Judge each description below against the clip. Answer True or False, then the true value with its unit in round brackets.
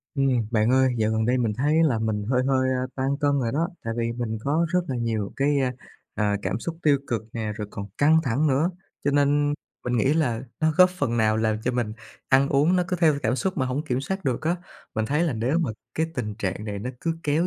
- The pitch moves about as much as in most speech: True (5.0 semitones)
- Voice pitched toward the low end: True (130 Hz)